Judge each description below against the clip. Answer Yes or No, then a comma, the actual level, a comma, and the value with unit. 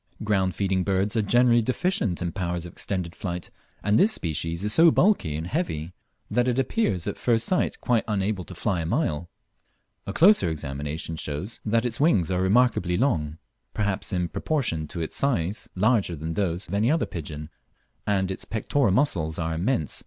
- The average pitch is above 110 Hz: No, very low, 95 Hz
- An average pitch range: No, wide, 5.9 semitones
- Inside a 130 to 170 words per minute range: No, average, 180 wpm